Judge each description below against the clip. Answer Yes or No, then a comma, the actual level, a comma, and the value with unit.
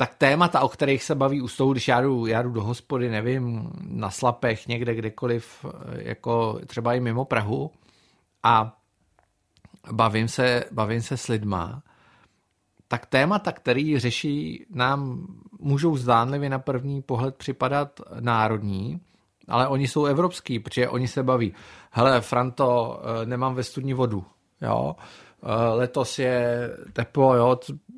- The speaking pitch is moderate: No, low, 125 Hz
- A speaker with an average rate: Yes, average, 135 wpm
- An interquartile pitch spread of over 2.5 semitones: Yes, average, 2.9 semitones